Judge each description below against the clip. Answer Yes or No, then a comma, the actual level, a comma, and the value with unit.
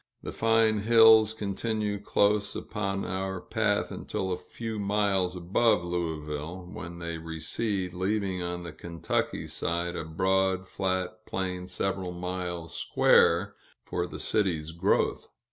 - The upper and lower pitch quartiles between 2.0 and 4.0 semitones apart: Yes, average, 2.8 semitones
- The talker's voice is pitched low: Yes, very low, 95 Hz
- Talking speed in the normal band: No, slow, 130 wpm